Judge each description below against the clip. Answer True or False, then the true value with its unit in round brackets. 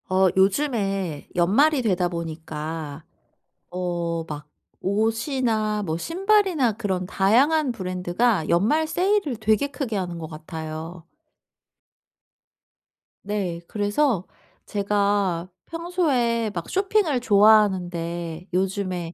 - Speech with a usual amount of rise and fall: False (6.0 semitones)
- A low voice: False (200 Hz)